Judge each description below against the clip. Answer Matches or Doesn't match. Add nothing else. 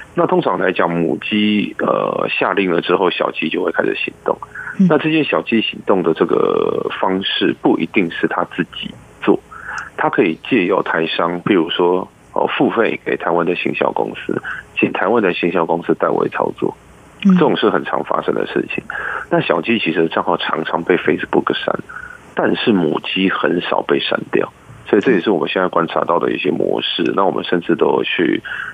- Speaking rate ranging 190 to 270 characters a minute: Doesn't match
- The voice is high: Matches